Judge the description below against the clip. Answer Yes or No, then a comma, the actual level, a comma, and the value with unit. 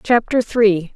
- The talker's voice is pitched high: Yes, high, 215 Hz